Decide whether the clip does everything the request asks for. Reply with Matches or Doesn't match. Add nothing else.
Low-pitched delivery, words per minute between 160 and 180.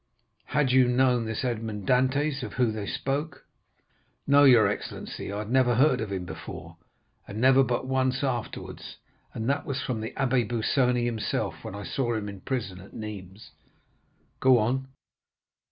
Matches